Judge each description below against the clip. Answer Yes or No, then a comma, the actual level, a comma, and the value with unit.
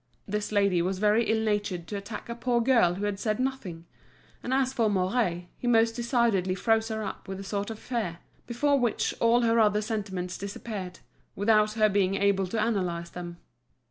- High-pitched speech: Yes, high, 210 Hz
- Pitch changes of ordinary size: Yes, average, 3.2 semitones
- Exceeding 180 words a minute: Yes, average, 190 wpm